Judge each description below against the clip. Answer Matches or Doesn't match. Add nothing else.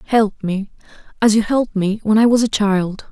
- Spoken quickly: Matches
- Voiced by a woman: Matches